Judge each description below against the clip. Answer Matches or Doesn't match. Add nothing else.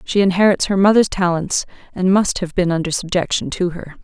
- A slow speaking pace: Doesn't match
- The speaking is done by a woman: Matches